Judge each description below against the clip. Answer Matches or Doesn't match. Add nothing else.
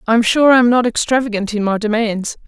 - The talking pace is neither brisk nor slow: Doesn't match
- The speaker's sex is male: Doesn't match